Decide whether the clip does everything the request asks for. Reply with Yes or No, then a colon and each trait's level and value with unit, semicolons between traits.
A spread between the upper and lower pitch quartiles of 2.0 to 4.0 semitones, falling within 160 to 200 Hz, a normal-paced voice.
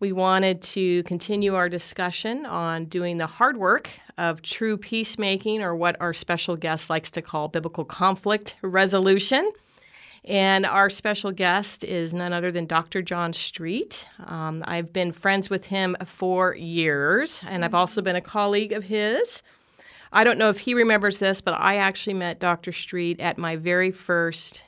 Yes: average, 2.8 semitones; medium, 185 Hz; average, 170 wpm